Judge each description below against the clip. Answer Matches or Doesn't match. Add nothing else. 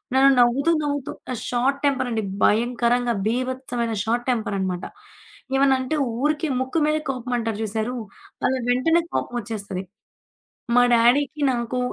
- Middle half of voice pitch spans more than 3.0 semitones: Doesn't match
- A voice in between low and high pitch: Doesn't match